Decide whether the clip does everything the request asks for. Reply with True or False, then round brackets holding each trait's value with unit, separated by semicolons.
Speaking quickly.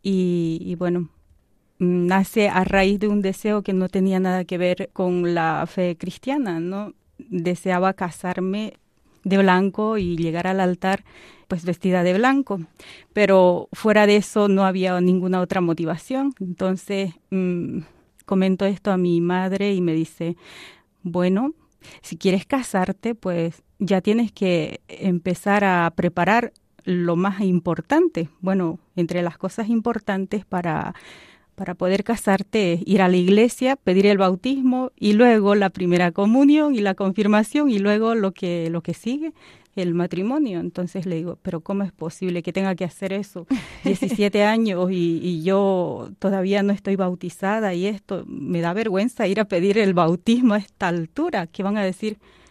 False (155 wpm)